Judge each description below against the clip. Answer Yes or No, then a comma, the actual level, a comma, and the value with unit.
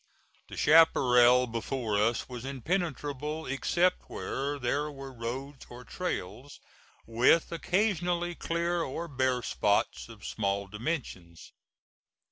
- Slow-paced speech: Yes, slow, 105 wpm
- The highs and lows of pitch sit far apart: Yes, wide, 5.7 semitones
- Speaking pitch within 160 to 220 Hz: No, low, 135 Hz